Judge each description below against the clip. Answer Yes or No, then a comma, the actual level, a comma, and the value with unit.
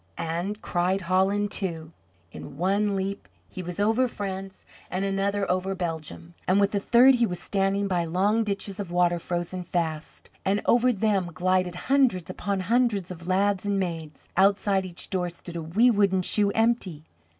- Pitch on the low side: No, high, 190 Hz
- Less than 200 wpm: Yes, average, 170 wpm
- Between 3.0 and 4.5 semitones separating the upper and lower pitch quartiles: No, narrow, 2.5 semitones